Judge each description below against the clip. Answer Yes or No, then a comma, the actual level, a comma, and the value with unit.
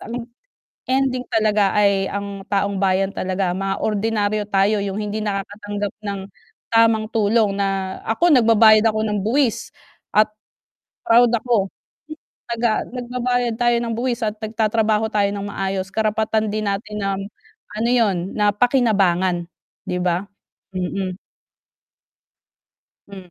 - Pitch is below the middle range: No, high, 210 Hz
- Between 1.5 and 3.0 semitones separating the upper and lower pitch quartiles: Yes, narrow, 2.4 semitones